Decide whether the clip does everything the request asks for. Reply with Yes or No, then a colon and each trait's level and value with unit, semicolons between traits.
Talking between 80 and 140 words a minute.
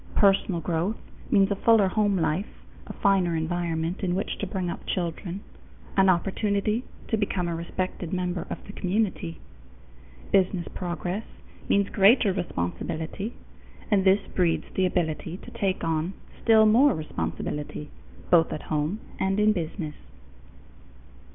Yes: slow, 135 wpm